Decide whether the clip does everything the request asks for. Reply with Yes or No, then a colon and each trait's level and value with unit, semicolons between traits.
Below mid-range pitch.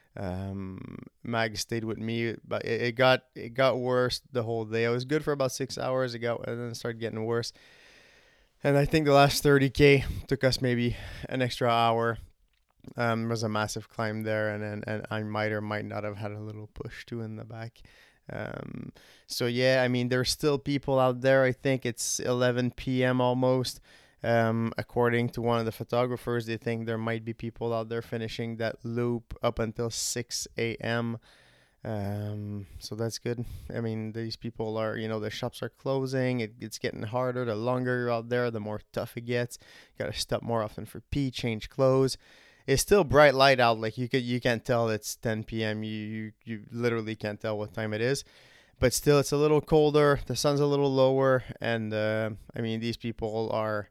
Yes: low, 115 Hz